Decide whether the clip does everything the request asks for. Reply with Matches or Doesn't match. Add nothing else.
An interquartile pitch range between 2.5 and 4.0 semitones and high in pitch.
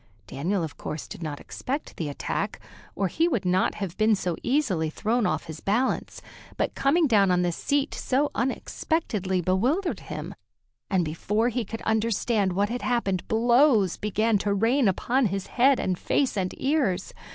Doesn't match